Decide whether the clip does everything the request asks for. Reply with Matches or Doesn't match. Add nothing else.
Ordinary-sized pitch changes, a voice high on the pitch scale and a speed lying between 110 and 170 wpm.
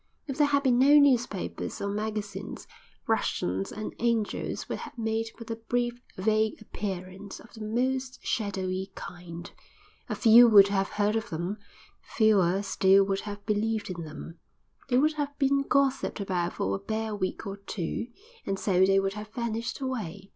Matches